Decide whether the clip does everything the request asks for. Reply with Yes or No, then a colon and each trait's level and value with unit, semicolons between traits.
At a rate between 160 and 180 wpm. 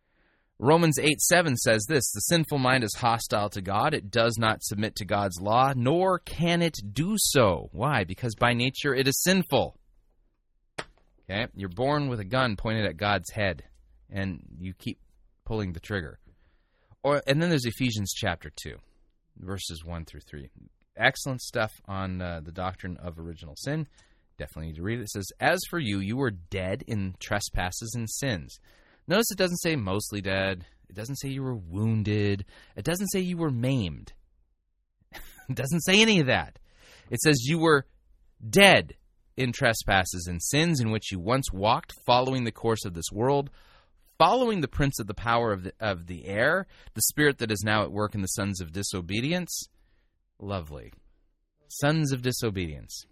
Yes: average, 175 wpm